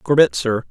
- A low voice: Yes, low, 125 Hz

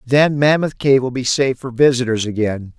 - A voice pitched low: Yes, low, 130 Hz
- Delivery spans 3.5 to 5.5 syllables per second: Yes, 5.3 syllables/s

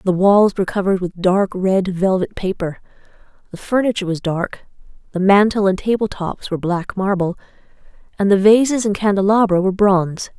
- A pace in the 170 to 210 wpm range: No, average, 160 wpm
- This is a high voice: Yes, high, 195 Hz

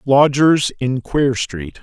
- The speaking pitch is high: No, low, 130 Hz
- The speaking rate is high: No, slow, 130 wpm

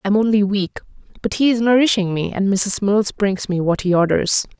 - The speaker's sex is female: Yes, female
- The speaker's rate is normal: No, fast, 220 wpm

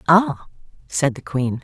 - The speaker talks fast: No, average, 145 wpm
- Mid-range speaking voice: Yes, medium, 150 Hz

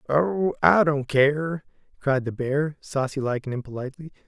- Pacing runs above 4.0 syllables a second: Yes, 4.6 syllables/s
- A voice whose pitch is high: No, medium, 140 Hz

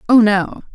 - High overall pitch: Yes, high, 215 Hz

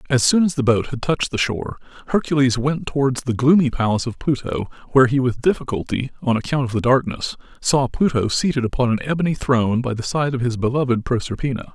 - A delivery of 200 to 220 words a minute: Yes, fast, 205 wpm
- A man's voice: Yes, male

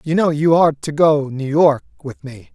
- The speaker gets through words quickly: Yes, fast, 235 wpm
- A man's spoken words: Yes, male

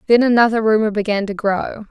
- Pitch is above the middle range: Yes, high, 215 Hz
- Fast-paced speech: No, average, 190 wpm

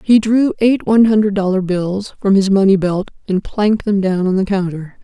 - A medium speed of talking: No, fast, 215 wpm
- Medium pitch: No, high, 200 Hz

